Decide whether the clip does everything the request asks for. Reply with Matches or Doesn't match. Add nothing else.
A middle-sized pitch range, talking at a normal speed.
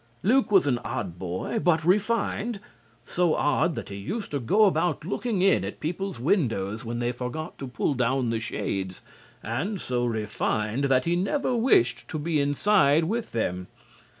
Doesn't match